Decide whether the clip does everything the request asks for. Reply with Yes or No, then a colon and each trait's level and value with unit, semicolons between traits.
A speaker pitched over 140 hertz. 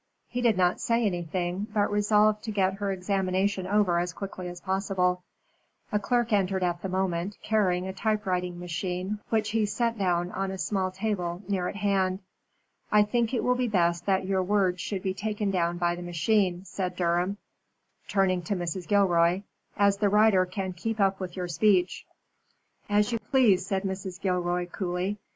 Yes: high, 190 Hz